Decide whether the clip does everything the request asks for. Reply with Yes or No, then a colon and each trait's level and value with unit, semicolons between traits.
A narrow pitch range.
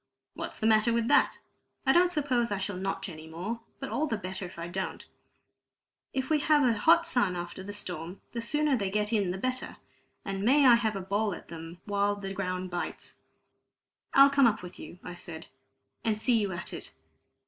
No: average, 5.1 semitones